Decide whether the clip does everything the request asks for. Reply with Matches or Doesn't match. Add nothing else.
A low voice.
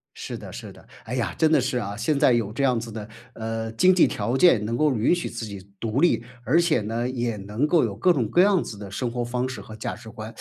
Matches